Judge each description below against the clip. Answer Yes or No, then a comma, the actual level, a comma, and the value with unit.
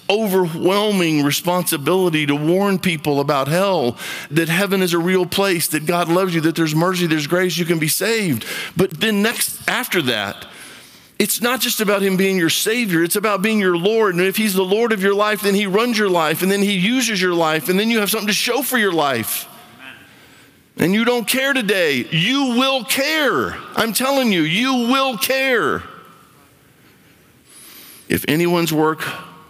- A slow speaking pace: No, average, 185 wpm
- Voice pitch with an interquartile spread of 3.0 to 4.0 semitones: No, average, 4.5 semitones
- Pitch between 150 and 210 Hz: Yes, high, 190 Hz